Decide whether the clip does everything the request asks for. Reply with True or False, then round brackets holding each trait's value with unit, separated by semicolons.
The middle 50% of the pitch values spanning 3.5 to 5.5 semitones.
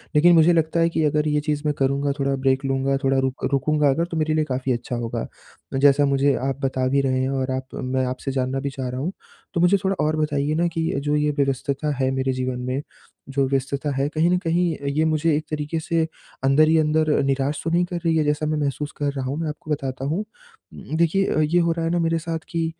False (3.1 semitones)